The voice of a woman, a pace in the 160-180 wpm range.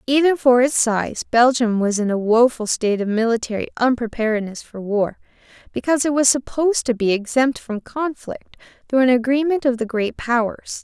Yes: female; average, 170 wpm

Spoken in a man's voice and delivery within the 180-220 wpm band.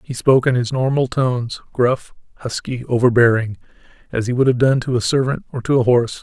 Yes: male; average, 200 wpm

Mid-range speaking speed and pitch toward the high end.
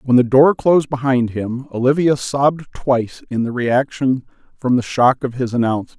No: average, 180 wpm; low, 130 Hz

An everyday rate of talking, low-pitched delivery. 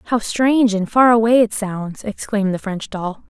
No: average, 195 wpm; high, 215 Hz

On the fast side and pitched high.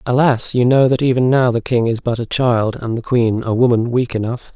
No: fast, 250 wpm; low, 120 Hz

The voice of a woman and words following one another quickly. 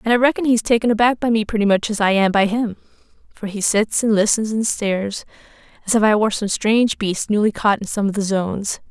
Yes: female; fast, 245 wpm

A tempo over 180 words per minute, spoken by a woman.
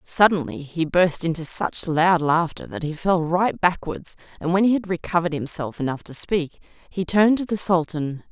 Yes: average, 190 wpm; female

